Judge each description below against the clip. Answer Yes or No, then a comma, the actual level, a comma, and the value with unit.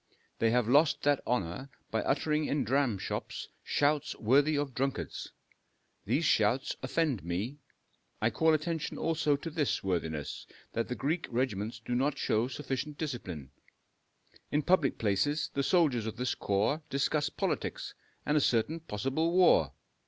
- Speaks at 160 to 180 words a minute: No, average, 145 wpm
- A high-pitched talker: No, low, 135 Hz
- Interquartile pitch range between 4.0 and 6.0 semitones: Yes, average, 4.9 semitones